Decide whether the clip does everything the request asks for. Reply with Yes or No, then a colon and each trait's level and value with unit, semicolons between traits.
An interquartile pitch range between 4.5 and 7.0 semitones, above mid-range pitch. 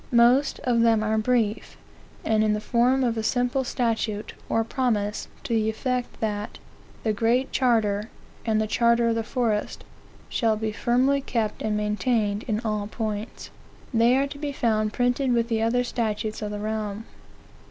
No: narrow, 2.4 semitones; high, 225 Hz